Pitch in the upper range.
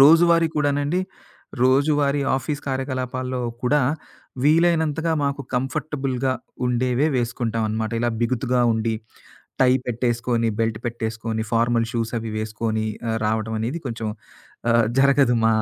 No: low, 125 Hz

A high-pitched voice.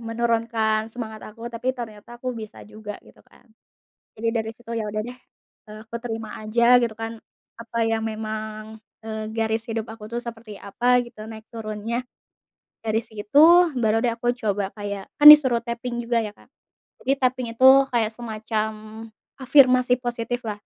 Yes: high, 225 Hz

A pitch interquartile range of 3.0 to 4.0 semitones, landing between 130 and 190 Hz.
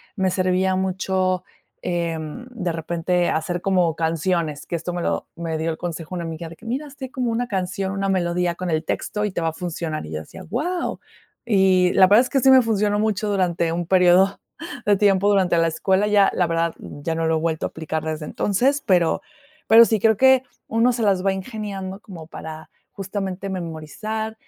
Yes: average, 3.7 semitones; medium, 185 Hz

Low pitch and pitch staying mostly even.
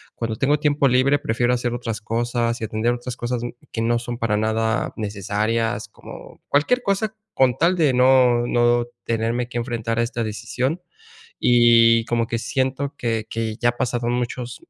Yes: low, 120 Hz; narrow, 1.8 semitones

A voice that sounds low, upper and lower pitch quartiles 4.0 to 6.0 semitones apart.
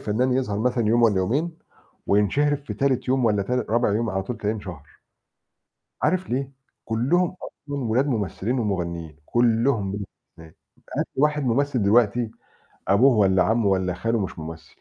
Yes: low, 115 Hz; average, 4.7 semitones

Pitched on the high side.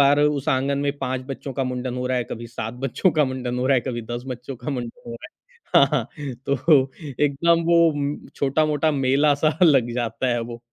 No: low, 135 Hz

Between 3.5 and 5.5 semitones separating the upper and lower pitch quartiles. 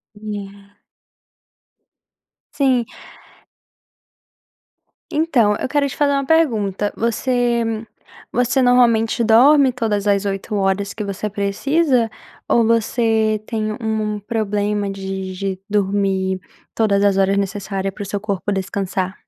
No: average, 3.0 semitones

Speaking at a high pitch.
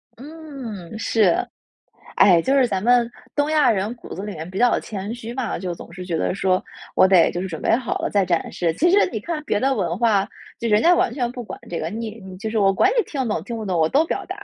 Yes: high, 220 Hz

